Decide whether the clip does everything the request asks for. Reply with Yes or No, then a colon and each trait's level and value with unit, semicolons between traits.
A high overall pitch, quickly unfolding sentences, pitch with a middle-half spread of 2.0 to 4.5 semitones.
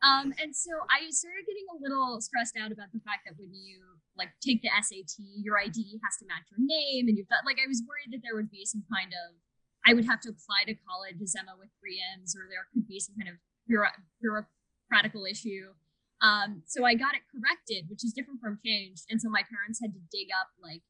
Yes: high, 215 Hz; fast, 235 wpm; average, 4.2 semitones